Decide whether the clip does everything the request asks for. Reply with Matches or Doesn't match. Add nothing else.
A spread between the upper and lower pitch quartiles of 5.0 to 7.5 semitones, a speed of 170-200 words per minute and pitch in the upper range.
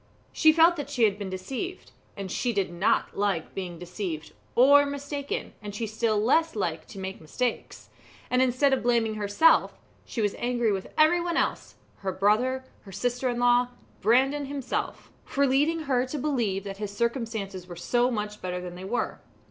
Matches